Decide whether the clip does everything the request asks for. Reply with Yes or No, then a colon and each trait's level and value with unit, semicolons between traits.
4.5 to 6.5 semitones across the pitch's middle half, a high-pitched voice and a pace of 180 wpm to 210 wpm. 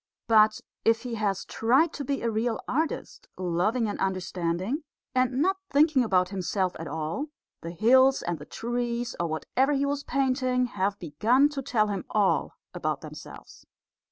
No: wide, 5.6 semitones; high, 230 Hz; average, 160 wpm